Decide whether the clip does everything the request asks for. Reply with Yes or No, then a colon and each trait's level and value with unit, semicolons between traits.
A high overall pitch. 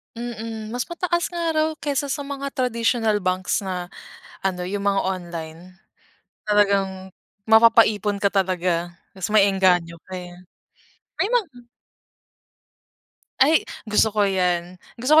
Yes: high, 205 Hz